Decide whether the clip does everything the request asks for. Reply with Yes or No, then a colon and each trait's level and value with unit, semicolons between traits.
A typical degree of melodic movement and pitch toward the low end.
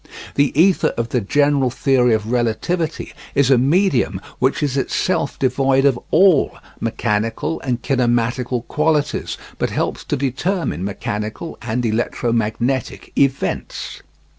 Yes: average, 3.6 semitones; low, 130 Hz